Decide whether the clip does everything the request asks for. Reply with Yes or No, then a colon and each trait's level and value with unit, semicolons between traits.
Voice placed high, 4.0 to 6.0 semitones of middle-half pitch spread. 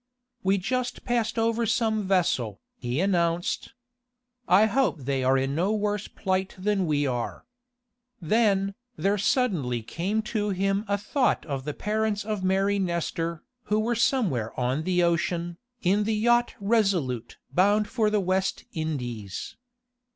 Yes: high, 195 Hz; average, 4.6 semitones